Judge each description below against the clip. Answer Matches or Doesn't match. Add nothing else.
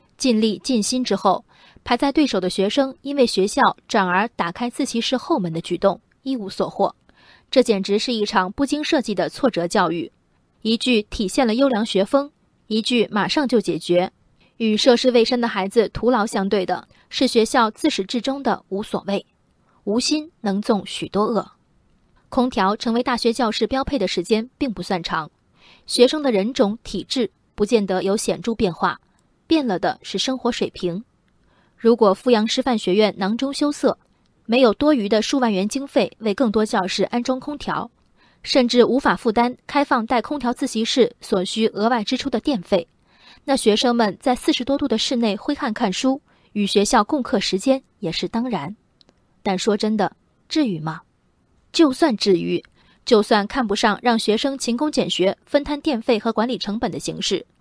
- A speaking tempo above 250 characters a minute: Matches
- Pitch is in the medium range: Doesn't match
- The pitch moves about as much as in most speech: Matches